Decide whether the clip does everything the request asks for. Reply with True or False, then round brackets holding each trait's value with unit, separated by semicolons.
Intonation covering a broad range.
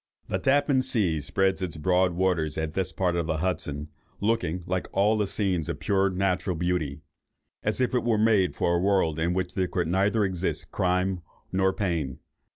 False (2.4 semitones)